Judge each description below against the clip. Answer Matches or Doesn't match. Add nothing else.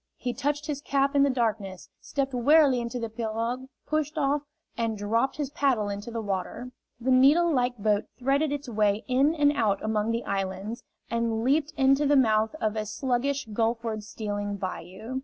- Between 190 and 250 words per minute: Doesn't match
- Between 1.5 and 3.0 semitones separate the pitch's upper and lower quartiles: Doesn't match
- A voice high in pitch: Matches